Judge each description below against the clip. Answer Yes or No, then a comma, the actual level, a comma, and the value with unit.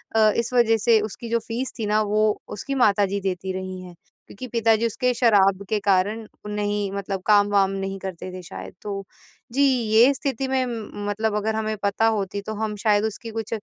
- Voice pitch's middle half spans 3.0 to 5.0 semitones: No, narrow, 2.4 semitones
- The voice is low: No, high, 210 Hz